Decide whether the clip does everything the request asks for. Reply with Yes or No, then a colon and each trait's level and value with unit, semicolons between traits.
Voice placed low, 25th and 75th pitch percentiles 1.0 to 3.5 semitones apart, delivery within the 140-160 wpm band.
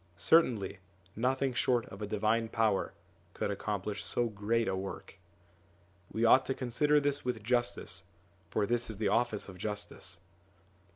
Yes: low, 110 Hz; average, 3.2 semitones; average, 150 wpm